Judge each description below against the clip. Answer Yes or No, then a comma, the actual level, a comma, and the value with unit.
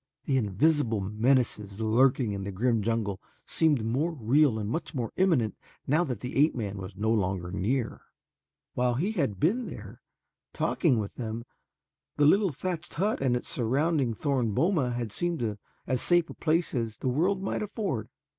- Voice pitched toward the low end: Yes, low, 125 Hz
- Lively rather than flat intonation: Yes, wide, 6.3 semitones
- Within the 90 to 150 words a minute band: No, average, 170 wpm